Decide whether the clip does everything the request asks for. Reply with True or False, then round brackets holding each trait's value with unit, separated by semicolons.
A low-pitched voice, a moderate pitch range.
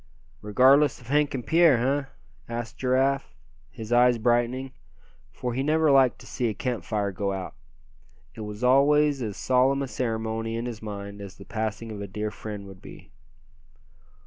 True (120 Hz; 4.0 semitones)